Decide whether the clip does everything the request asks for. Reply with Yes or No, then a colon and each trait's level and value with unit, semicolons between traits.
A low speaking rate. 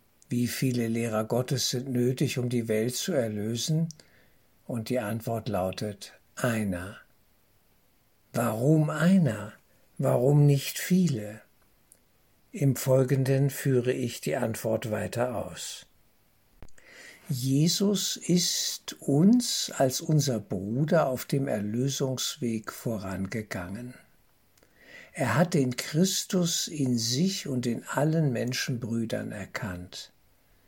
Yes: slow, 100 wpm